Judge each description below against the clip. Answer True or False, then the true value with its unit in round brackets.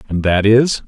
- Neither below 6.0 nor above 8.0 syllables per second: False (4.4 syllables/s)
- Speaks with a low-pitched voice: True (110 Hz)